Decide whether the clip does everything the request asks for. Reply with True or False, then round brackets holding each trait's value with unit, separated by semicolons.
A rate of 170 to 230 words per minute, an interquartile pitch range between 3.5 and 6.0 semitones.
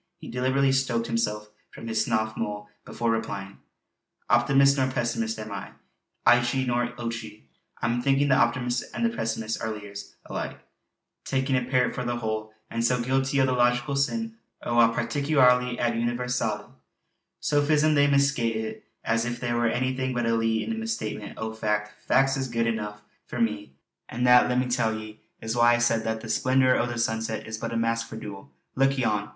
False (190 wpm; 2.6 semitones)